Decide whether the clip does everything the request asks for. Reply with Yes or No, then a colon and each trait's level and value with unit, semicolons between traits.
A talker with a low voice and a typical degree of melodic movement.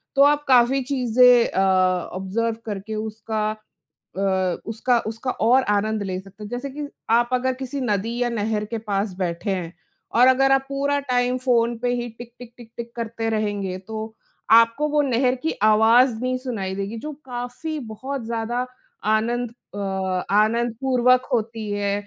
No: high, 230 Hz; average, 3.1 semitones